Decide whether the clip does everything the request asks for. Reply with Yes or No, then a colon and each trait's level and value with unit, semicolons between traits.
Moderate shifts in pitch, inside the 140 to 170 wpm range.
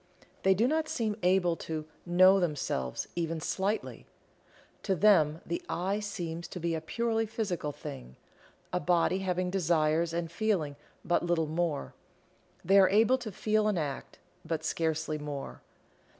Yes: average, 3.9 semitones; average, 150 wpm